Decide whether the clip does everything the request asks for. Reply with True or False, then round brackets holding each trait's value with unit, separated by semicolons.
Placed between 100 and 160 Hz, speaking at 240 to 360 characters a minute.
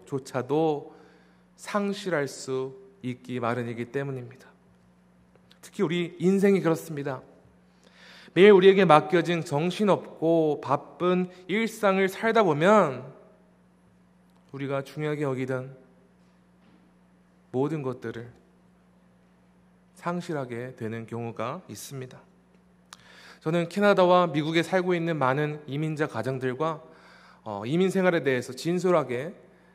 False (140 Hz; 230 characters per minute)